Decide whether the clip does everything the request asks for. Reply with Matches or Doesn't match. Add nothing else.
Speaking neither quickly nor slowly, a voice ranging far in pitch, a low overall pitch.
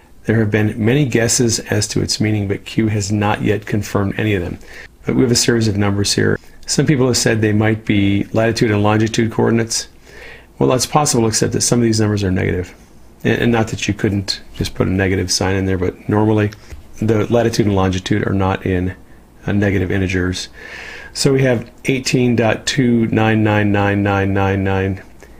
Doesn't match